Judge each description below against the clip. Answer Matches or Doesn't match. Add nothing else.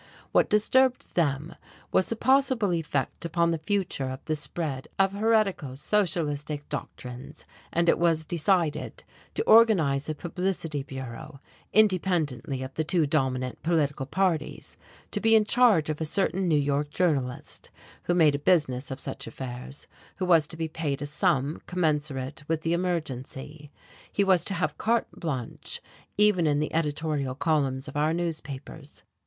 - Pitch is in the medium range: Matches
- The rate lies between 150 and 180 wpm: Matches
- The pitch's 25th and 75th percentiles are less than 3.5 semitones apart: Doesn't match